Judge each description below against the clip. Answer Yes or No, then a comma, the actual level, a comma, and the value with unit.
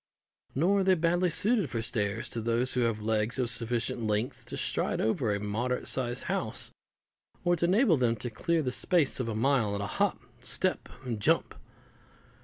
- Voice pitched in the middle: No, low, 125 Hz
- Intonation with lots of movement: Yes, wide, 7.0 semitones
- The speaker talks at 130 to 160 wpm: No, average, 190 wpm